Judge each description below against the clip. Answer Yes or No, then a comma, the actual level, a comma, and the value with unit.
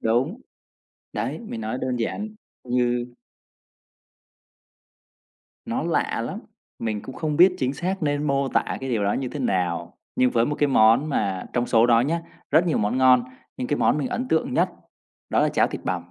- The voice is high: No, low, 130 Hz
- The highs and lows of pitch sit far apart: No, average, 4.6 semitones